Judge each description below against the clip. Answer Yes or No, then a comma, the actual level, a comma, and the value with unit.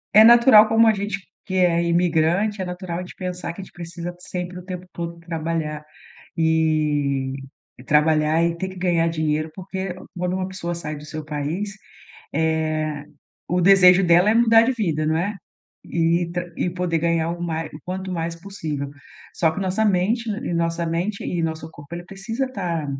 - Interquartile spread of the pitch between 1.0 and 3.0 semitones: Yes, average, 2.7 semitones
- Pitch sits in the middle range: Yes, medium, 175 Hz